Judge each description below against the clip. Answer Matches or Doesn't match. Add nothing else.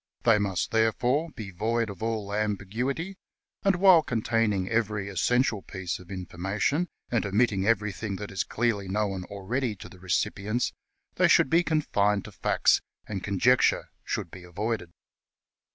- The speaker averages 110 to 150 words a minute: Matches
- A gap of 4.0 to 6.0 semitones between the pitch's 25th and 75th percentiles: Doesn't match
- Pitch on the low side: Matches